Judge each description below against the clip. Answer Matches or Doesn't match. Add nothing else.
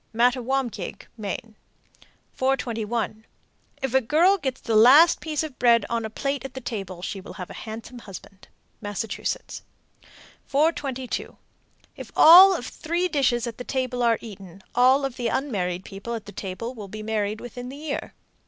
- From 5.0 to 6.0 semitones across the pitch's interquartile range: Doesn't match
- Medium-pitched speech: Doesn't match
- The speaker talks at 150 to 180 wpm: Matches